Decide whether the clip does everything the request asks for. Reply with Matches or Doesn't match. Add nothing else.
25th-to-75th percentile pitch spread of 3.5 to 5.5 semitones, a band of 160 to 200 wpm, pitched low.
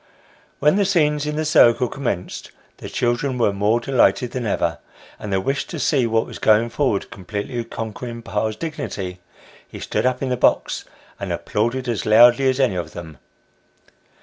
Matches